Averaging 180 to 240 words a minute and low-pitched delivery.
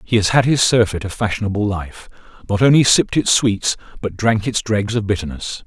Yes: average, 200 wpm; low, 105 Hz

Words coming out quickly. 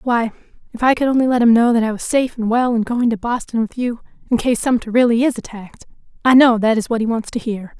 Yes: fast, 270 wpm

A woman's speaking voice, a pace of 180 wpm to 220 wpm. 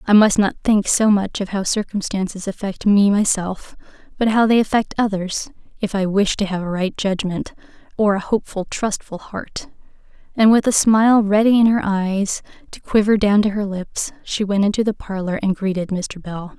Yes: female; average, 190 wpm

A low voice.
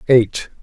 Yes: low, 120 Hz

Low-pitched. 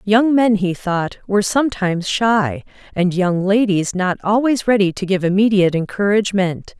No: high, 200 Hz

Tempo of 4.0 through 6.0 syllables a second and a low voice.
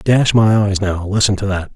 Yes: 5.0 syllables/s; low, 100 Hz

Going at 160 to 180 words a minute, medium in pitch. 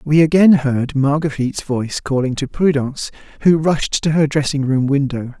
Yes: average, 165 wpm; medium, 145 Hz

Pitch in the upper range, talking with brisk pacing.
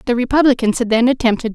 Yes: high, 240 Hz; fast, 235 wpm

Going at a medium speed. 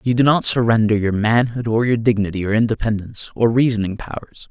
Yes: average, 185 wpm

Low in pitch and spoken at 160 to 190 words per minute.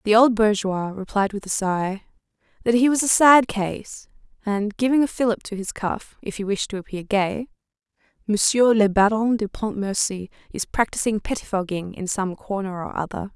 No: high, 210 Hz; average, 175 wpm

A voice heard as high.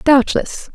Yes: very high, 270 Hz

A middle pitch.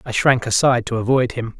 No: low, 120 Hz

